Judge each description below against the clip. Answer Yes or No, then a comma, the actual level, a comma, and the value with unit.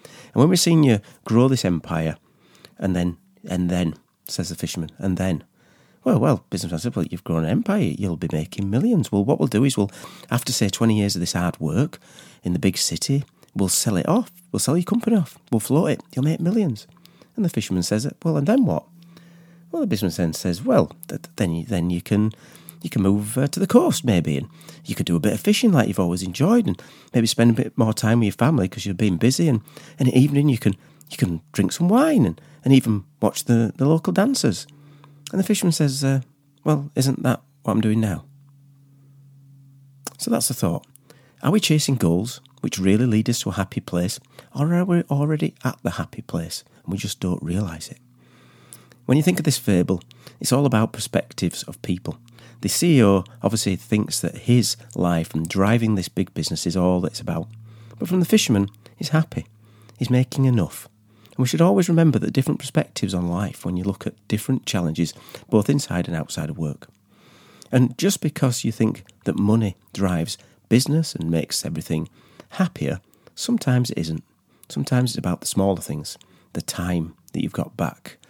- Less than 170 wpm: No, fast, 205 wpm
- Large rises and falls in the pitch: Yes, wide, 7.0 semitones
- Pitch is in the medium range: No, low, 115 Hz